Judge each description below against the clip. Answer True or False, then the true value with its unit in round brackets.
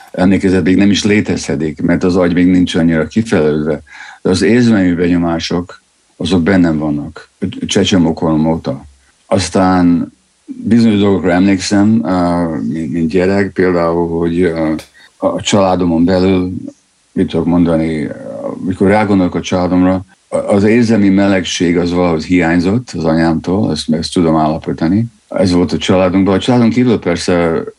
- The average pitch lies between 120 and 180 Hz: False (90 Hz)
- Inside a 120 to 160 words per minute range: True (125 wpm)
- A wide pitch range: False (2.5 semitones)